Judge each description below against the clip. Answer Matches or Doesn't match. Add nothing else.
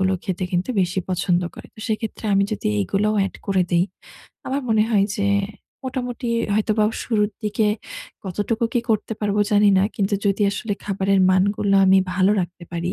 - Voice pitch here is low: Doesn't match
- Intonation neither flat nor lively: Doesn't match